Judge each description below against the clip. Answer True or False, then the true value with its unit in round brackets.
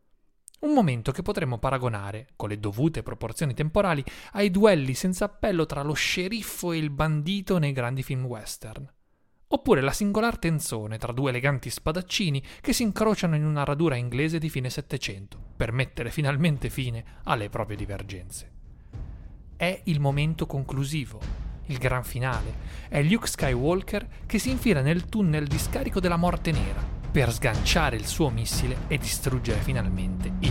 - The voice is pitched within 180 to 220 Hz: False (140 Hz)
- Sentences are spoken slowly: False (155 wpm)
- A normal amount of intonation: False (5.9 semitones)